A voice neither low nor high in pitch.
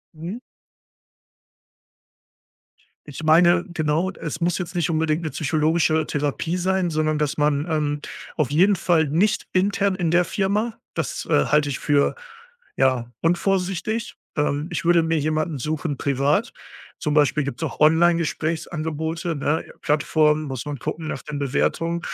Yes: medium, 160 Hz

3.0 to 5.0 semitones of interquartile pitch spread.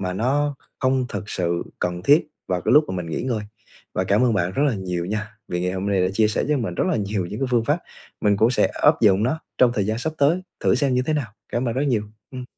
No: wide, 5.6 semitones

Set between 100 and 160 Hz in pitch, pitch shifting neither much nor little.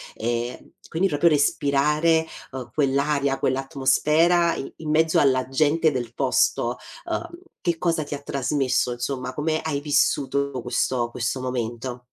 Yes: medium, 140 Hz; average, 3.3 semitones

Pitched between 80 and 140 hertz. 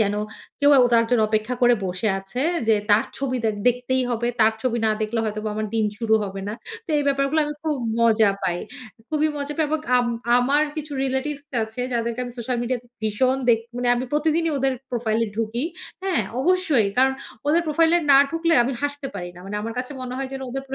No: very high, 250 Hz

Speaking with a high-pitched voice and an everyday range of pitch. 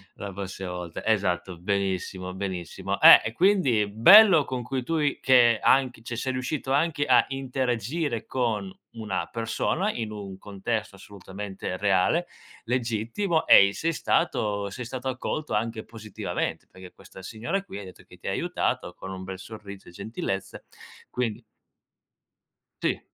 No: low, 110 Hz; average, 5.0 semitones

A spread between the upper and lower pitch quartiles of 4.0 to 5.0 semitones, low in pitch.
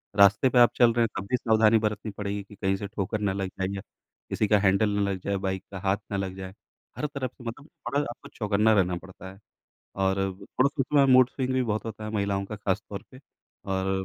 No: average, 3.3 semitones; low, 105 Hz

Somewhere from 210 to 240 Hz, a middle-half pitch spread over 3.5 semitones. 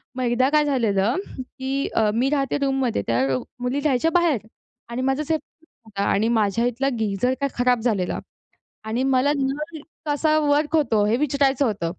No: very high, 260 Hz; average, 3.9 semitones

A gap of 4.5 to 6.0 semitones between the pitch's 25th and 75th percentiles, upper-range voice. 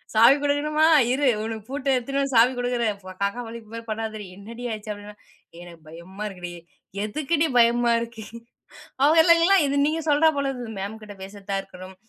Yes: average, 5.2 semitones; high, 230 Hz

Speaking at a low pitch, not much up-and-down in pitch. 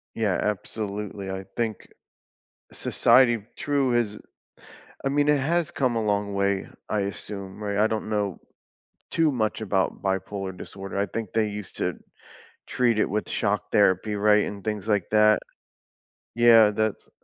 Yes: low, 105 Hz; narrow, 2.3 semitones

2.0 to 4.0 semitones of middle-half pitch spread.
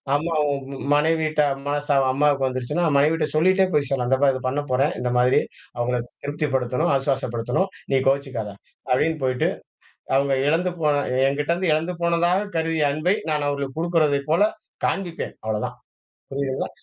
Yes: average, 3.3 semitones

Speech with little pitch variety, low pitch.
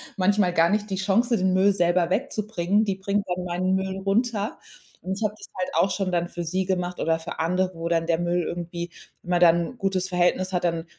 No: narrow, 2.1 semitones; medium, 185 Hz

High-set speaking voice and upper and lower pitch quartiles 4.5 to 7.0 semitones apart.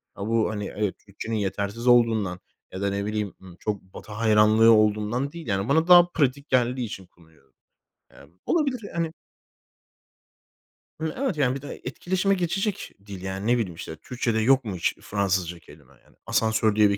No: low, 110 Hz; average, 5.0 semitones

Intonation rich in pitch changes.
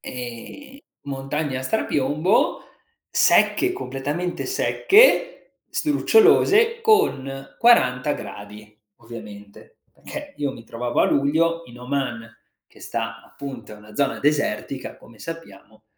Yes: wide, 6.8 semitones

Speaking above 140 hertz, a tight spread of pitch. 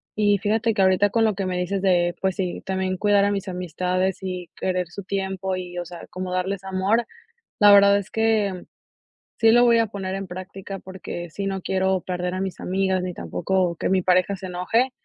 Yes: high, 190 Hz; narrow, 1.6 semitones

